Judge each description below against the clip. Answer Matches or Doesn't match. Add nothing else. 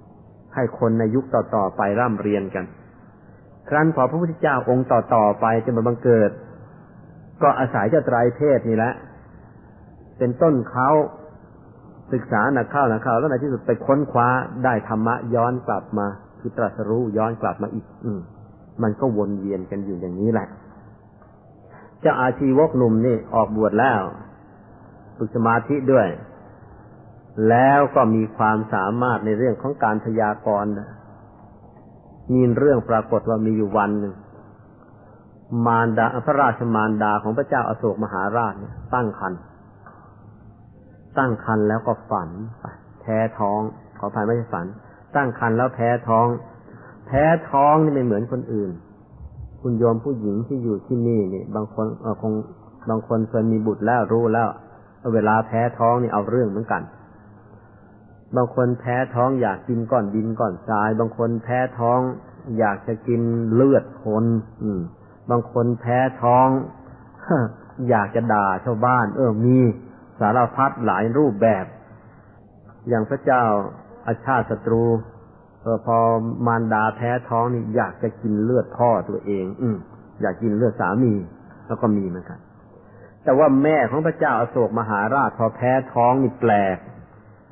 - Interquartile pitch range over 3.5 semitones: Doesn't match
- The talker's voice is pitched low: Matches